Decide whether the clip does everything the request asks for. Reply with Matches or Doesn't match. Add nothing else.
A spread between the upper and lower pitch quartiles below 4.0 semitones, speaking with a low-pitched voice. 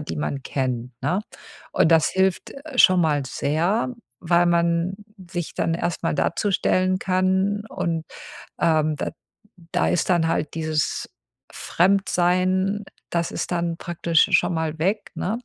Doesn't match